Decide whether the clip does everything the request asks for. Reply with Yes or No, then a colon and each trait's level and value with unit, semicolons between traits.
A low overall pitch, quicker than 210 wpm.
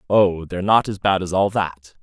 Yes: very low, 95 Hz; fast, 235 wpm